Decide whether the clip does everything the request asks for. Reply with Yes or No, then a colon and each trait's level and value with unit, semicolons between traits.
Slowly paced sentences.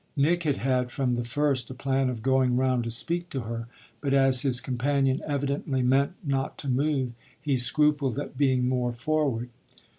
No: average, 180 wpm